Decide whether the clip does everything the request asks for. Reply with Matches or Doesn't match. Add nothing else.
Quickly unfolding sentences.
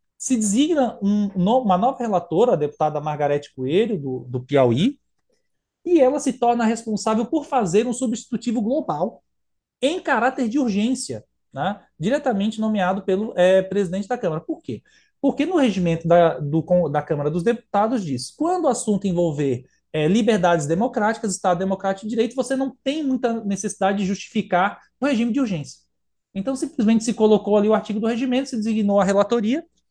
Doesn't match